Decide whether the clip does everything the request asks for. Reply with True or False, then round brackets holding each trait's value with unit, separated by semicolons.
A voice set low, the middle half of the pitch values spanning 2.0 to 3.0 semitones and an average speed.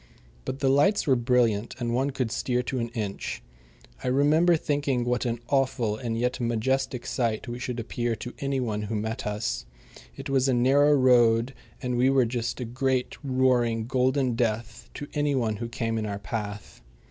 True (125 Hz; 2.6 semitones; 185 wpm)